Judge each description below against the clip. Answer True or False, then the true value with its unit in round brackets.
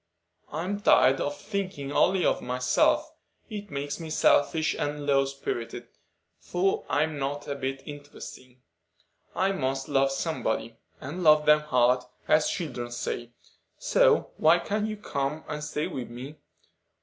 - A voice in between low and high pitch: True (145 Hz)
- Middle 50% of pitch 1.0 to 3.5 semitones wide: True (3.0 semitones)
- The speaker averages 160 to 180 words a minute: False (140 wpm)